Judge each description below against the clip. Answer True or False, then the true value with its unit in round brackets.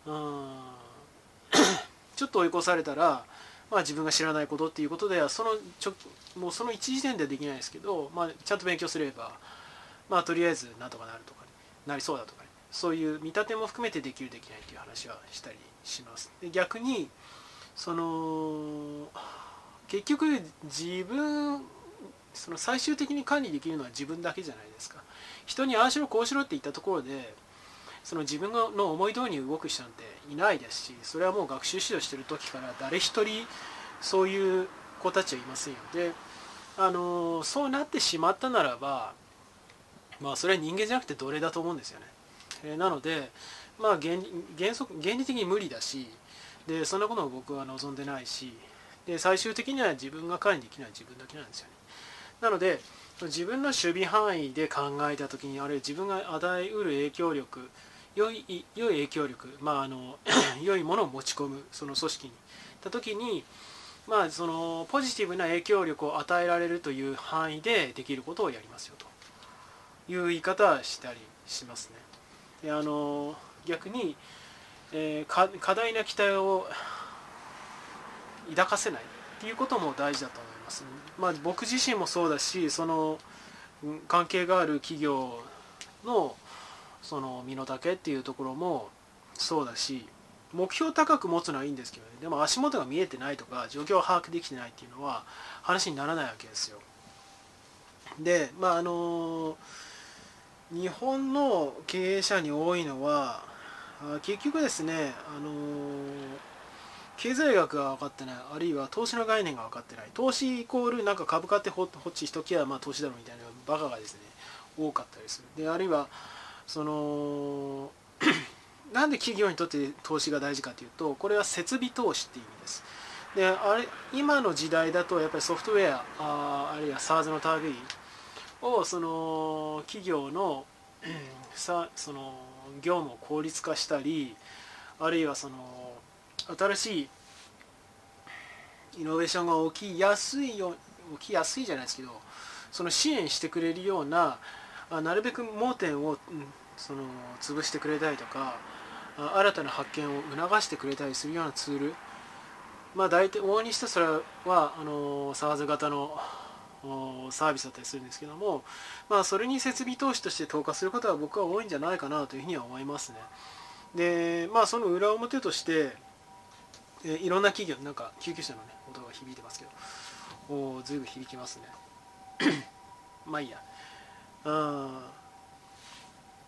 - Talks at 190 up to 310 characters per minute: False (320 characters per minute)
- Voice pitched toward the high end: False (165 Hz)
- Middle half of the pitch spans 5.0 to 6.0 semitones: True (5.4 semitones)